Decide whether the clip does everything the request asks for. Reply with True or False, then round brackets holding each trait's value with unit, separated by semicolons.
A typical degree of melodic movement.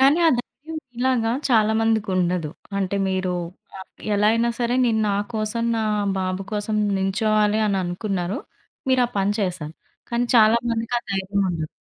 True (3.4 semitones)